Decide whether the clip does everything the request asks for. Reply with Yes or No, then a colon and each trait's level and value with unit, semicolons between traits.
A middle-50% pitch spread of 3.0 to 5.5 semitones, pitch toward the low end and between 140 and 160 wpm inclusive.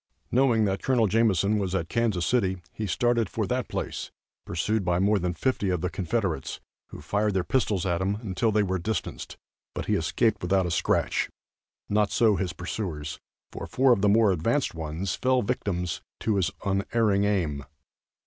No: average, 3.7 semitones; low, 100 Hz; average, 175 wpm